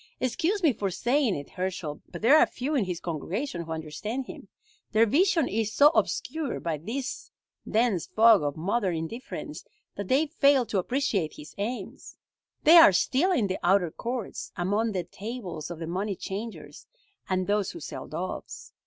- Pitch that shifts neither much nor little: No, wide, 6.3 semitones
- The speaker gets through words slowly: No, average, 170 wpm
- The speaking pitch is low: No, high, 210 Hz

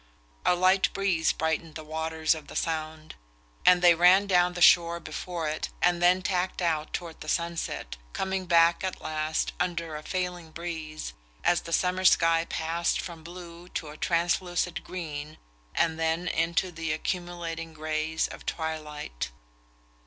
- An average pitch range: No, narrow, 2.0 semitones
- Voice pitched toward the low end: No, medium, 170 Hz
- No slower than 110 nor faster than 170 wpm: Yes, average, 150 wpm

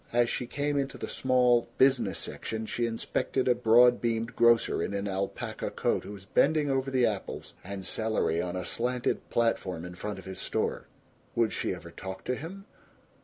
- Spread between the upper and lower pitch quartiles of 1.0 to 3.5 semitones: No, average, 4.2 semitones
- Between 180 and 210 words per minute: Yes, average, 185 wpm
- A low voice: Yes, low, 115 Hz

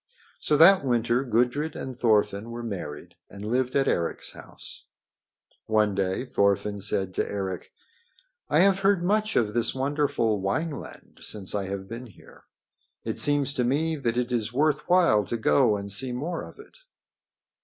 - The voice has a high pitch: No, low, 120 Hz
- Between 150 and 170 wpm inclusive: Yes, average, 165 wpm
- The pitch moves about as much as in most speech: No, wide, 6.0 semitones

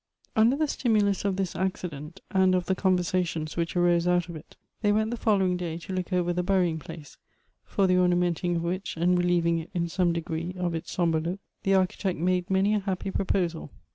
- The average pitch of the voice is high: No, medium, 180 Hz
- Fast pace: Yes, fast, 220 wpm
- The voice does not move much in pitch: Yes, narrow, 2.0 semitones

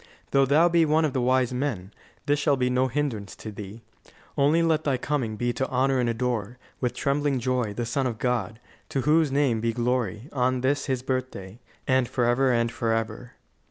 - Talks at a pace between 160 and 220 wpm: Yes, average, 195 wpm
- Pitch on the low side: Yes, low, 125 Hz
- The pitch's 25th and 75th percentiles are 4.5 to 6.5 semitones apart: No, average, 2.9 semitones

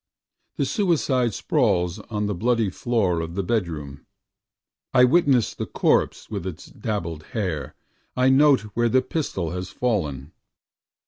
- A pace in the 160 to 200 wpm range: No, slow, 135 wpm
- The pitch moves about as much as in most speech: No, wide, 6.4 semitones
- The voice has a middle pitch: No, low, 105 Hz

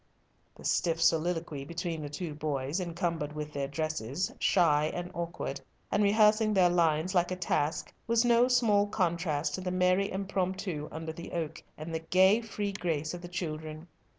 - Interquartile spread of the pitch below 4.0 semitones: Yes, average, 3.3 semitones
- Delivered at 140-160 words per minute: No, average, 170 wpm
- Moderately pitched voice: Yes, medium, 170 Hz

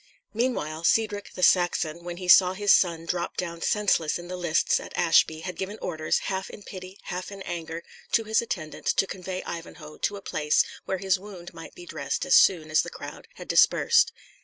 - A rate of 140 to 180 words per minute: No, average, 200 wpm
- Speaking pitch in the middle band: Yes, medium, 180 Hz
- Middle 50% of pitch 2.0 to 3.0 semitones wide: Yes, narrow, 2.6 semitones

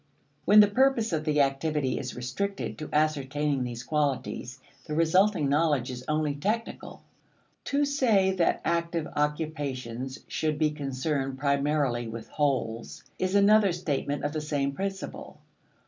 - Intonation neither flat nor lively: Yes, average, 4.3 semitones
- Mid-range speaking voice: Yes, medium, 150 Hz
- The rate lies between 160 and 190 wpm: No, slow, 135 wpm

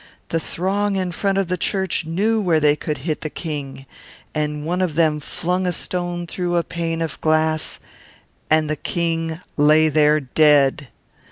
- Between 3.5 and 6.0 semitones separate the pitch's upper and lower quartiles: No, average, 2.8 semitones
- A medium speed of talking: Yes, average, 170 wpm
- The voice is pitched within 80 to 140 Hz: No, medium, 165 Hz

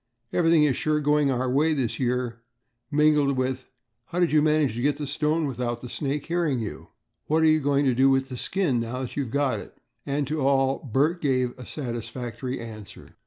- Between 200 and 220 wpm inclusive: Yes, fast, 205 wpm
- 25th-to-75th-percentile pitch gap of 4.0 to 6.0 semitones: No, average, 3.1 semitones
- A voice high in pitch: No, low, 135 Hz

